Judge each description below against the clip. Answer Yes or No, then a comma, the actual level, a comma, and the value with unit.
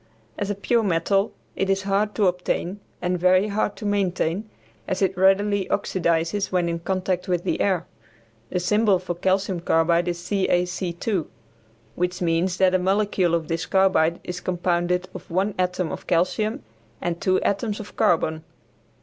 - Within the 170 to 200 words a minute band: No, average, 160 wpm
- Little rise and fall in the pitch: Yes, narrow, 2.2 semitones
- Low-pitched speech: No, medium, 185 Hz